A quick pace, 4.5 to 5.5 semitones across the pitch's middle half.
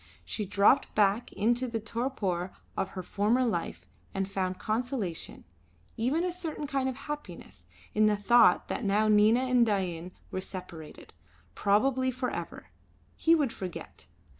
No: average, 145 wpm; average, 4.9 semitones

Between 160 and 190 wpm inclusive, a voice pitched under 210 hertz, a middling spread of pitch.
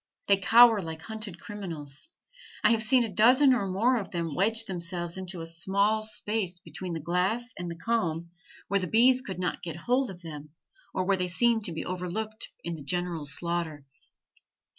Yes: average, 185 wpm; medium, 185 Hz; average, 4.4 semitones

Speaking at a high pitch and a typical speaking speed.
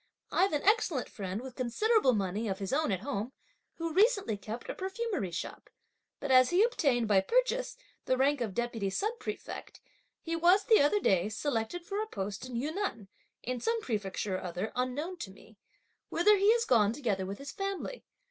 Yes: very high, 260 Hz; average, 185 wpm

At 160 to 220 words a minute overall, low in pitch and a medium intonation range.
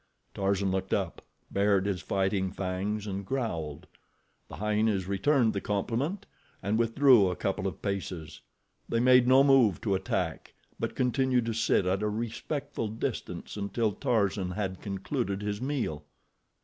No: average, 145 wpm; low, 105 Hz; average, 3.7 semitones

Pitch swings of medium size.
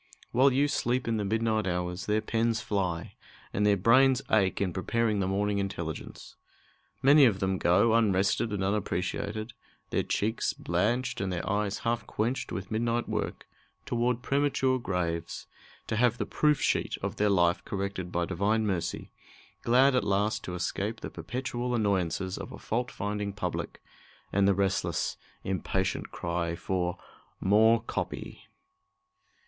Yes: average, 3.8 semitones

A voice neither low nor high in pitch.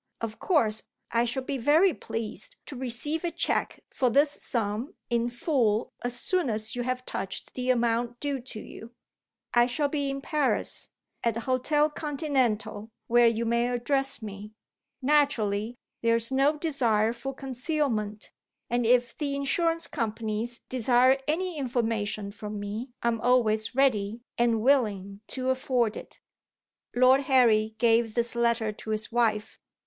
No: high, 240 Hz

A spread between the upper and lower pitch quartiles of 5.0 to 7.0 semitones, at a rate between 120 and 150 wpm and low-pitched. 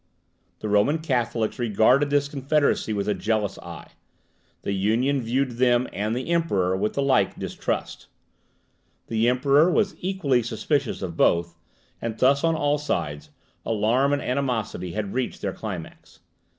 Yes: average, 5.3 semitones; average, 145 wpm; low, 120 Hz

